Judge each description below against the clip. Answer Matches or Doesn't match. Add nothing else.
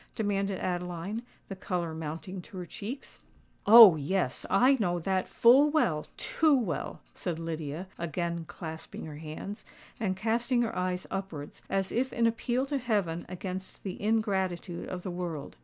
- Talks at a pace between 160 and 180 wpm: Doesn't match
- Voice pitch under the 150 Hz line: Doesn't match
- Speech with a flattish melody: Doesn't match